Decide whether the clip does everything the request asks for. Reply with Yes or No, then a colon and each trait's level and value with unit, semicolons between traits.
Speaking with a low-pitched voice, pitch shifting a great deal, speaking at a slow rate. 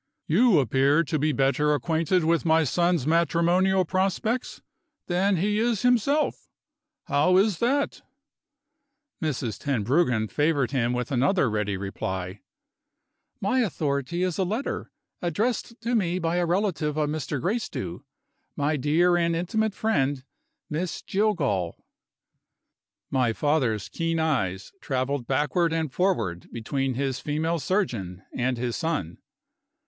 No: medium, 160 Hz; wide, 5.7 semitones; slow, 125 wpm